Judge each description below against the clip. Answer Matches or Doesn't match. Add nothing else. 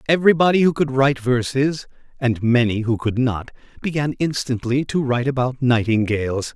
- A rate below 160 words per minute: Matches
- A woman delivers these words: Doesn't match